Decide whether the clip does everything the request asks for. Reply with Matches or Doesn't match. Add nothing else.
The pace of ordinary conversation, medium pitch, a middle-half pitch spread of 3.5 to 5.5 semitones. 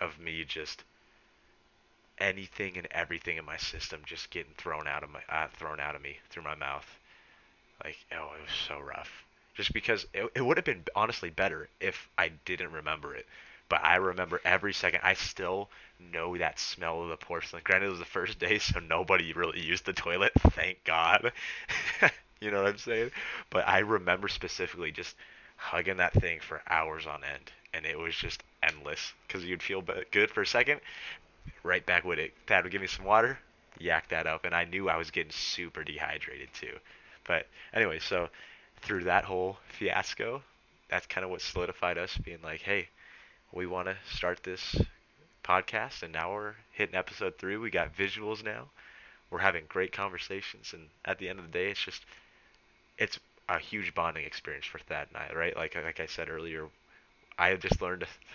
Doesn't match